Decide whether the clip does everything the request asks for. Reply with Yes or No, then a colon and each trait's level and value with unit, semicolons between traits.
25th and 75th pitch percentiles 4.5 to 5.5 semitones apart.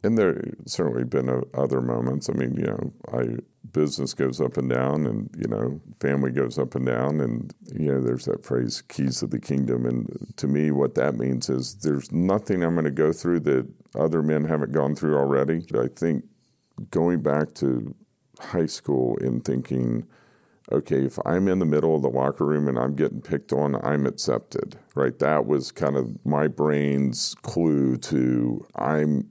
No: average, 2.9 semitones